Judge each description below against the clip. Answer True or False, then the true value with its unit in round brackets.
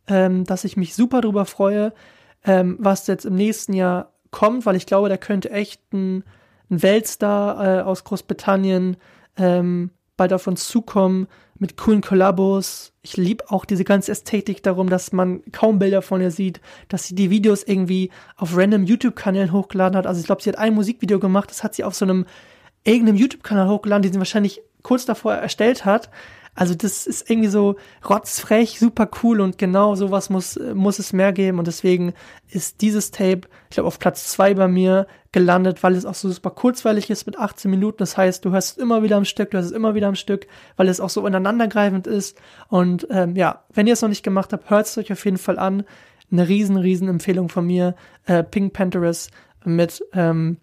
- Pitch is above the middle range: True (195 Hz)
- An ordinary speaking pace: False (205 wpm)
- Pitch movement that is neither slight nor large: False (2.0 semitones)